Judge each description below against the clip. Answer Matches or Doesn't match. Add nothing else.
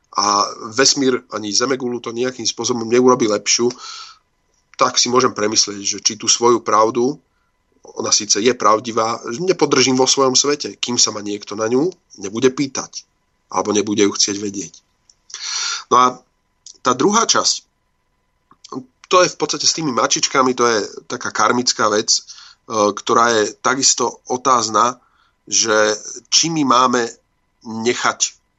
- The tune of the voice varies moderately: Matches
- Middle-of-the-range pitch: Doesn't match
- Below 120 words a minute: Doesn't match